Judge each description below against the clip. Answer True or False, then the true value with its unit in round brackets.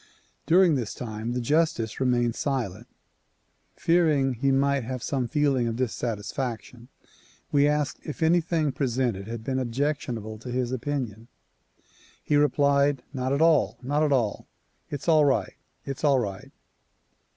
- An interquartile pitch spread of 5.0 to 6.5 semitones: False (3.6 semitones)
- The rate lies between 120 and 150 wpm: True (140 wpm)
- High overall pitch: False (130 Hz)